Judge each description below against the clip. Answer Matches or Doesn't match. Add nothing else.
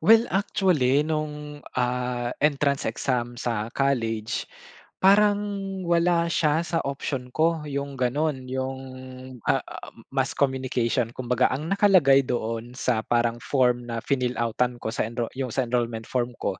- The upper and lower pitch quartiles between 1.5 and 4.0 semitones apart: Matches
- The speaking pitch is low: Matches